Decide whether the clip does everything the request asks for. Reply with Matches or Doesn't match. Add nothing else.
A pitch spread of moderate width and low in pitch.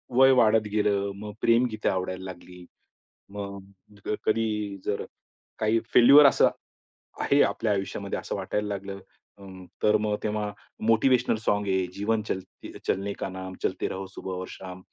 Doesn't match